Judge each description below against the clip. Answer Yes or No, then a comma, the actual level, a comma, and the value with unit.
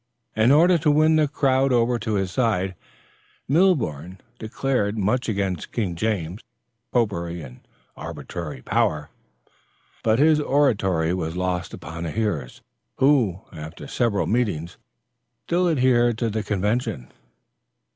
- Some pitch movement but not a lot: No, wide, 6.7 semitones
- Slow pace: Yes, slow, 125 wpm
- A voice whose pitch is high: No, low, 110 Hz